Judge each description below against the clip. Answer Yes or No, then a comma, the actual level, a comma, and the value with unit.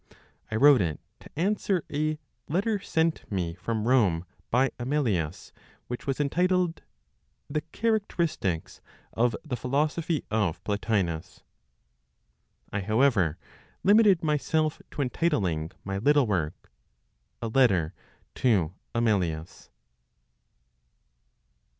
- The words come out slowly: Yes, slow, 100 wpm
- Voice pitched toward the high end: No, low, 125 Hz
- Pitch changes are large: Yes, wide, 8.3 semitones